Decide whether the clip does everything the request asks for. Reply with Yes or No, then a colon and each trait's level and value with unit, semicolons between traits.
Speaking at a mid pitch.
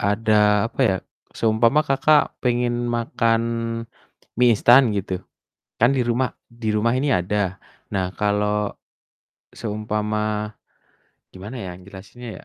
No: low, 110 Hz